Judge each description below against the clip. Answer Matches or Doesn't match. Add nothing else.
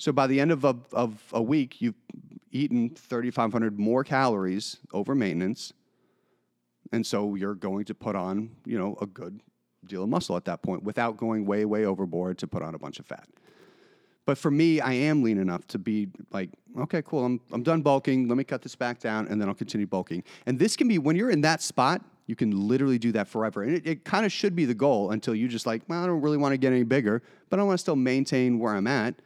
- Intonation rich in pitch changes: Matches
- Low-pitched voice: Matches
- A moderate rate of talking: Doesn't match